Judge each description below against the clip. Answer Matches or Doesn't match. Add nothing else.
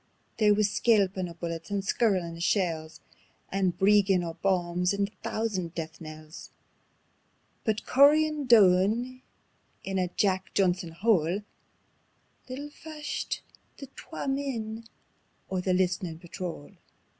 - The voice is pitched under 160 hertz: Doesn't match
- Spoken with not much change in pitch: Doesn't match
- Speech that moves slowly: Matches